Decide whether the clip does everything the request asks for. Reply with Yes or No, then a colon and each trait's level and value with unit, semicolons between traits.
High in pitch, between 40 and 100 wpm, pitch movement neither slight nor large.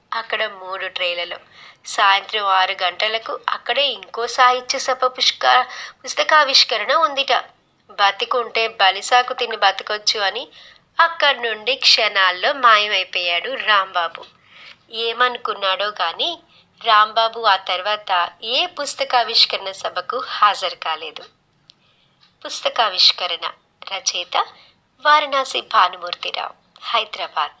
Yes: high, 220 Hz; average, 80 wpm; average, 5.0 semitones